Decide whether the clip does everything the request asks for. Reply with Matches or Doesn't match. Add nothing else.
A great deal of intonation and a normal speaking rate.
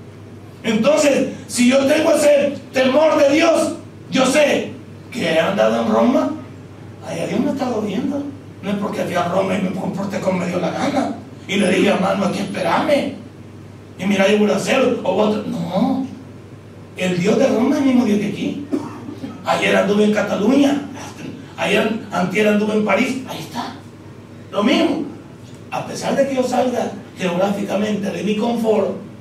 Matches